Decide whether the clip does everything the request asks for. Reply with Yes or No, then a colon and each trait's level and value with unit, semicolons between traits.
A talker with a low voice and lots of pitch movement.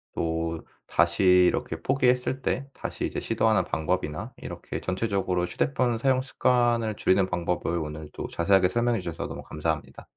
Yes: very low, 95 Hz; wide, 5.9 semitones